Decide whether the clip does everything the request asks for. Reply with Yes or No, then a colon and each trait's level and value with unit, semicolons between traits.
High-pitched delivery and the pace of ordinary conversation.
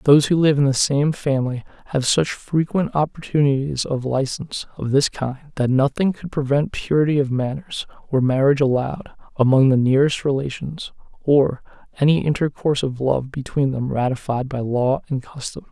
No: medium, 140 Hz; average, 160 wpm